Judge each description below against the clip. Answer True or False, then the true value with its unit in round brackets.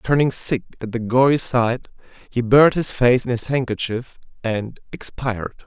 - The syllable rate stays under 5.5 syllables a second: True (4.7 syllables/s)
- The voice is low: True (120 Hz)